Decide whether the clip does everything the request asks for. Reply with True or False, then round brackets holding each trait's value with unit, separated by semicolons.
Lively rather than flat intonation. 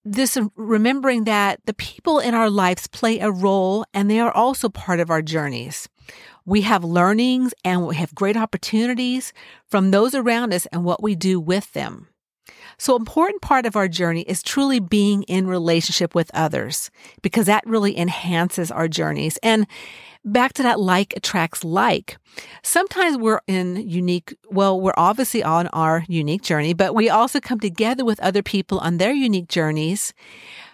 False (4.6 semitones)